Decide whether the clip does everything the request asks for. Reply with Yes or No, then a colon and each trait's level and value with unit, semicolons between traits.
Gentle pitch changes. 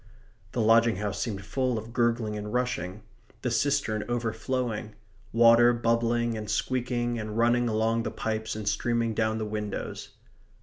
Yes: narrow, 1.8 semitones